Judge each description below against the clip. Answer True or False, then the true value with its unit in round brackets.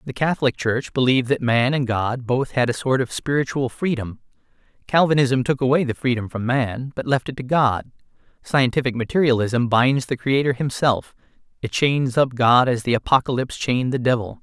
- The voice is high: False (130 Hz)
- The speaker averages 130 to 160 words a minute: False (180 wpm)